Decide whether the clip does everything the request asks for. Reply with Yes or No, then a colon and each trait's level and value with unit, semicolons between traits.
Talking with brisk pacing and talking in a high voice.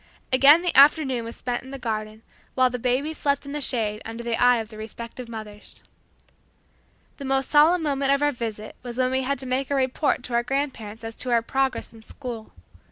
Yes: fast, 215 wpm; very high, 255 Hz